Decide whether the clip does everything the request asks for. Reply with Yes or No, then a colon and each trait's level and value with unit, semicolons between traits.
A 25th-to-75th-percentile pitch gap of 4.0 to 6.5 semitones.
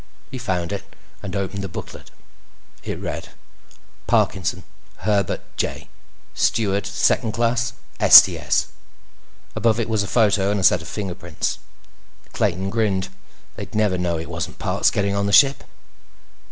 No: average, 2.7 semitones